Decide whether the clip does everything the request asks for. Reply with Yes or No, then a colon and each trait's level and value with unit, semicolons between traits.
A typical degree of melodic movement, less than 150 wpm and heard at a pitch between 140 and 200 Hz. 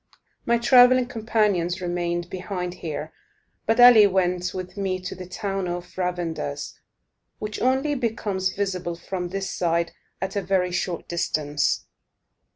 Yes: average, 3.2 semitones; slow, 135 wpm; medium, 185 Hz